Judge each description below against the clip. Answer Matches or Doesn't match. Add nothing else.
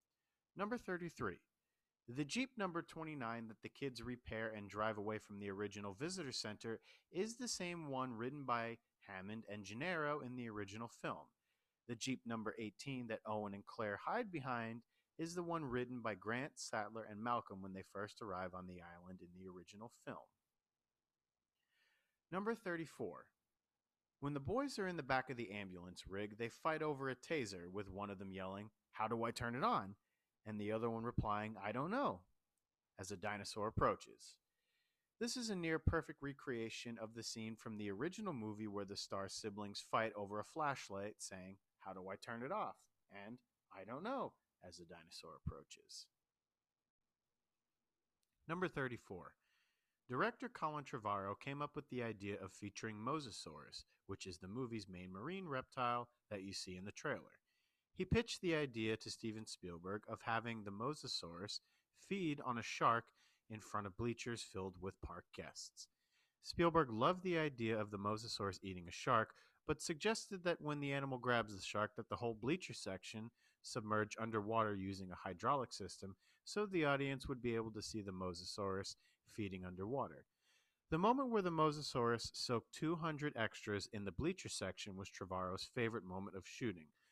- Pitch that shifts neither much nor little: Doesn't match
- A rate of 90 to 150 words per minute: Doesn't match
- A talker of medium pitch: Doesn't match